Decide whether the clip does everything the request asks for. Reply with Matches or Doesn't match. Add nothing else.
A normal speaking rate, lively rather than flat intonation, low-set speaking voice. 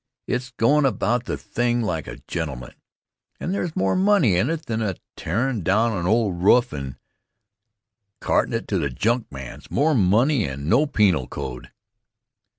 Matches